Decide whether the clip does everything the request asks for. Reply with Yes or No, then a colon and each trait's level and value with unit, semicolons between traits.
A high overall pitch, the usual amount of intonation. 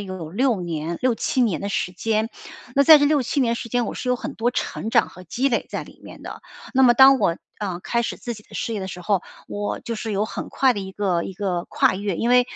Yes: high, 220 Hz; average, 4.5 semitones